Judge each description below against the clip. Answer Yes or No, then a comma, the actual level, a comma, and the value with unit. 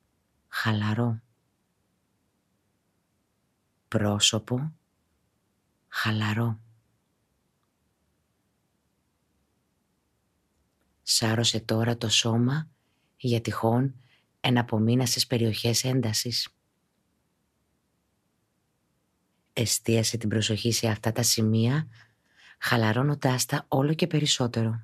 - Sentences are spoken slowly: Yes, slow, 60 wpm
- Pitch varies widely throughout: No, narrow, 2.3 semitones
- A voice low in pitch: Yes, low, 115 Hz